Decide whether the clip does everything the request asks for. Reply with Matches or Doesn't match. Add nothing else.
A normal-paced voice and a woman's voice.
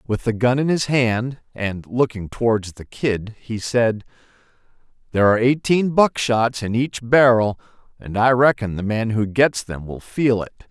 Doesn't match